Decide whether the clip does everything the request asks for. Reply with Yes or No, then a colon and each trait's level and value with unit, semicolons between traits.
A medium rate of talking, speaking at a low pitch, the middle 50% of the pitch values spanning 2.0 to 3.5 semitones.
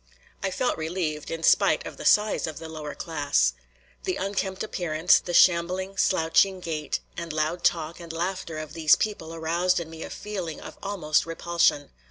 No: average, 175 wpm; medium, 170 Hz; average, 2.7 semitones